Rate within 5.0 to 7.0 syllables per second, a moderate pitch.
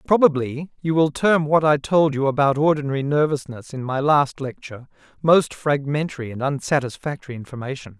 Yes: 5.5 syllables/s; medium, 145 Hz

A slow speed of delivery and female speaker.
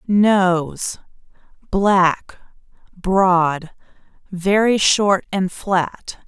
Yes: slow, 55 wpm; female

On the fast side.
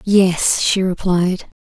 No: slow, 110 wpm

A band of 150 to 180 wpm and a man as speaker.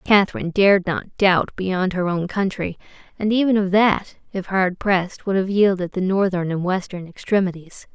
No: average, 175 wpm; female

